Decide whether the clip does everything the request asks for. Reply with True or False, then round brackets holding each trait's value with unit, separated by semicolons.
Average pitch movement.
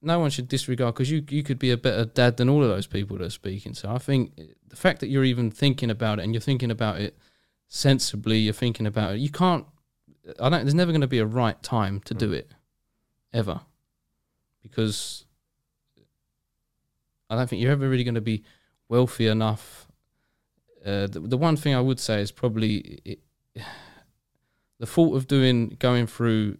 True (3.7 semitones)